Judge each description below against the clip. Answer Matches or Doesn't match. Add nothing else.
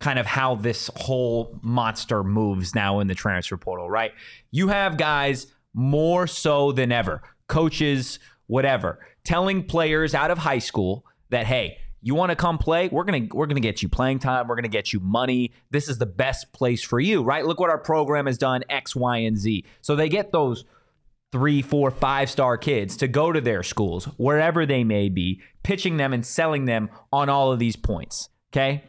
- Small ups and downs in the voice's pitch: Doesn't match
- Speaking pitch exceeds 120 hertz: Matches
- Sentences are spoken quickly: Doesn't match